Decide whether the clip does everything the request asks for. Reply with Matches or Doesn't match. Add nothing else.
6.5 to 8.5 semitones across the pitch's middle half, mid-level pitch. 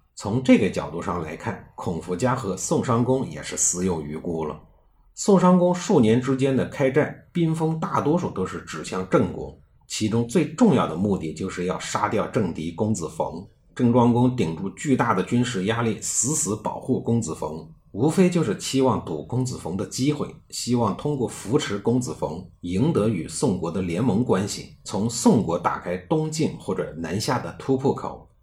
Doesn't match